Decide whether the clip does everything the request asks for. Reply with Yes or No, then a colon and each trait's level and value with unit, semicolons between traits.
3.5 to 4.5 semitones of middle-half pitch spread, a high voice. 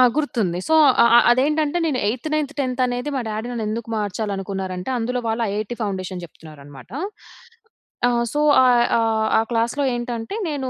Yes: average, 4.2 semitones; high, 230 Hz